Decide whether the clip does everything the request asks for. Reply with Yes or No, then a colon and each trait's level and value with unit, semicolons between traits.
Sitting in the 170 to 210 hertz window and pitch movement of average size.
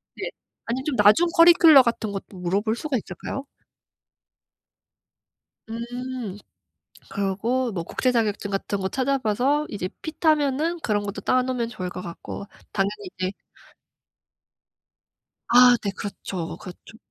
No: high, 230 Hz; average, 4.6 semitones